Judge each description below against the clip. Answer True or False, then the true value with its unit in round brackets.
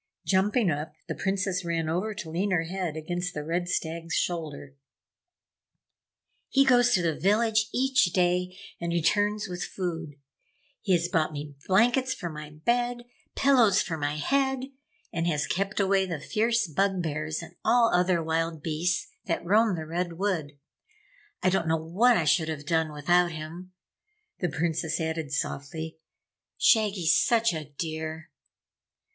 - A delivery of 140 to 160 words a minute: True (150 wpm)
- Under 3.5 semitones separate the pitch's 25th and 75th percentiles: False (4.0 semitones)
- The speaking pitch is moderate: True (175 Hz)